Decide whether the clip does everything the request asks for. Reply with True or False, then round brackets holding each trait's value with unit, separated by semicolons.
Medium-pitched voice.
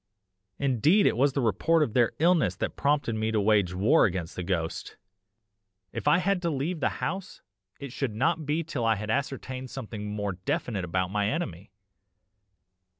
False (120 Hz)